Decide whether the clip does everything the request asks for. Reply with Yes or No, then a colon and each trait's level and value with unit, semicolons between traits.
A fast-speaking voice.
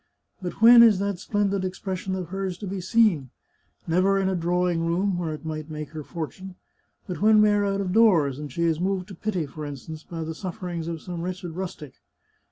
Yes: fast, 215 wpm